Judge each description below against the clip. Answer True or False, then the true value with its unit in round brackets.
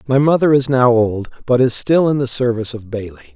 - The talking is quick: True (230 wpm)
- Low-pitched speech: True (125 Hz)